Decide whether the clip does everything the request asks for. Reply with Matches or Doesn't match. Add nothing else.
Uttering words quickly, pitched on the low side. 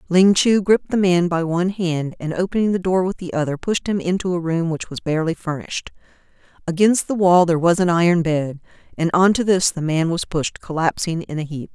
Doesn't match